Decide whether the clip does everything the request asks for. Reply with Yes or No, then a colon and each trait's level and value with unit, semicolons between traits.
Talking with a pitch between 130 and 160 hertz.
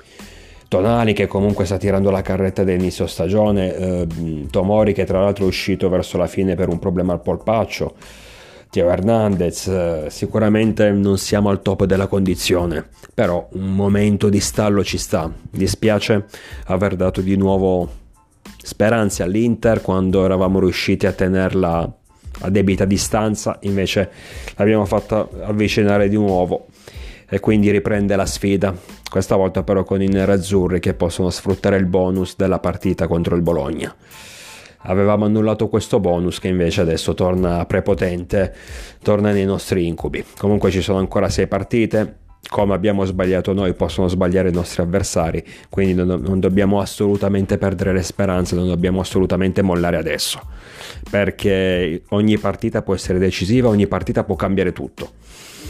No: very low, 95 Hz